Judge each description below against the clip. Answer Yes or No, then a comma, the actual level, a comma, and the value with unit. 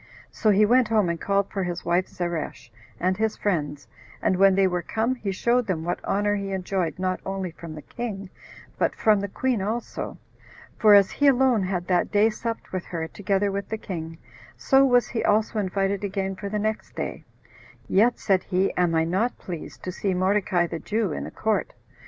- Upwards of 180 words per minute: Yes, average, 200 wpm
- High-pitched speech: Yes, high, 195 Hz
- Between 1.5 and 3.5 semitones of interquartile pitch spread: Yes, average, 2.9 semitones